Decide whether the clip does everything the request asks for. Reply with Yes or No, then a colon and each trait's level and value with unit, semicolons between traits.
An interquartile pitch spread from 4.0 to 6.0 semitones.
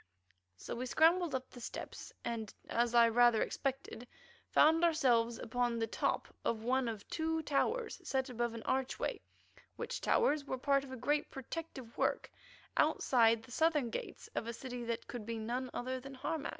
No: average, 3.4 semitones